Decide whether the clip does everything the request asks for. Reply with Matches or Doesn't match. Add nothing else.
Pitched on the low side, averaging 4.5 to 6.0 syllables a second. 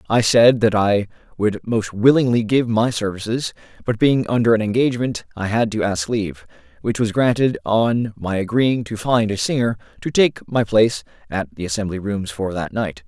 Matches